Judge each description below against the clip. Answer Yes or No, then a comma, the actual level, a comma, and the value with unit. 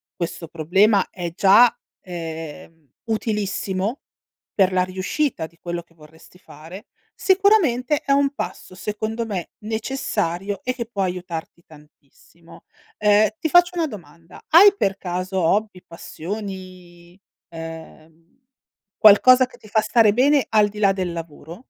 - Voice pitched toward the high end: Yes, high, 195 Hz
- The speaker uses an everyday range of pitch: Yes, average, 4.7 semitones